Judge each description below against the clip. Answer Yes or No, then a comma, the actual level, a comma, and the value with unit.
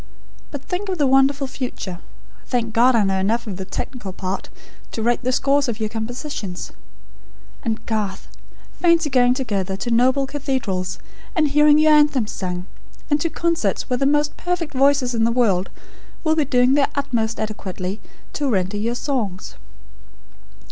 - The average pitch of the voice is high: Yes, high, 245 Hz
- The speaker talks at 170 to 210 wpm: No, average, 160 wpm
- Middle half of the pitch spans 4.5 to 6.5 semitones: Yes, average, 5.2 semitones